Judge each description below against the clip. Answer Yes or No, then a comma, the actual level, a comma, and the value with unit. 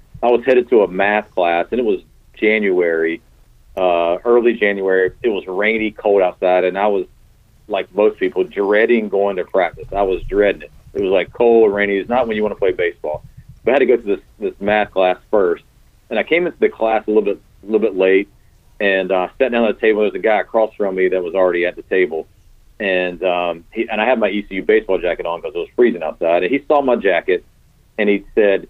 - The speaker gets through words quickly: Yes, fast, 245 wpm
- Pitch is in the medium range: No, low, 105 Hz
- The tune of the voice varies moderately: No, wide, 6.0 semitones